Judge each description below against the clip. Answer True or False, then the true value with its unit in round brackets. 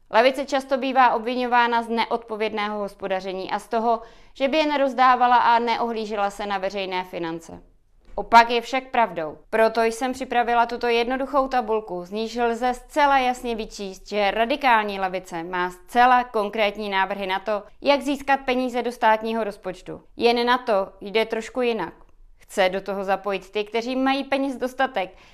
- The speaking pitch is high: True (225 Hz)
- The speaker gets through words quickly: False (155 wpm)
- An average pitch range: True (3.9 semitones)